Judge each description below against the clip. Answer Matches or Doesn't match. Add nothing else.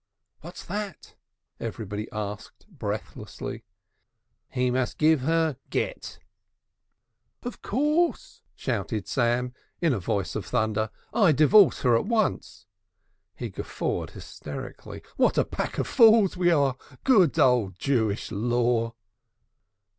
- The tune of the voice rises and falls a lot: Matches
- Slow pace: Matches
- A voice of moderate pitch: Doesn't match